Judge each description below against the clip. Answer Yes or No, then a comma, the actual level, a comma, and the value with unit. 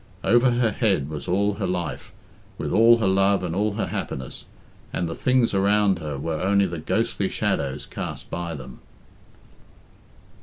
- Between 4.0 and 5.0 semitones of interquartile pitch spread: Yes, average, 4.4 semitones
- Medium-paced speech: Yes, average, 160 wpm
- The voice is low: Yes, very low, 95 Hz